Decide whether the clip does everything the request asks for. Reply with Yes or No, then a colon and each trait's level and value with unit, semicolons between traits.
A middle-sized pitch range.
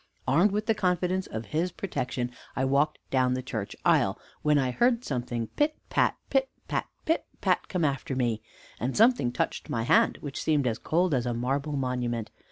No: wide, 6.6 semitones